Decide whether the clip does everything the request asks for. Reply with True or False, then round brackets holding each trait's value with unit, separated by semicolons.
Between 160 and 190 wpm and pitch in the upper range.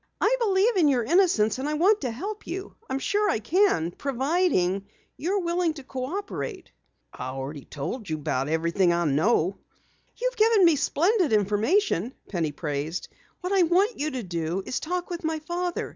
True (185 wpm; 285 Hz)